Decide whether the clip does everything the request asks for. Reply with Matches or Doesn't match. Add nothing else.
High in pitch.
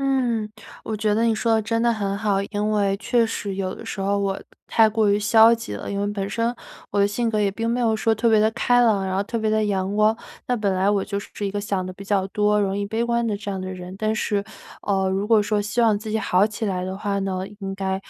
Matches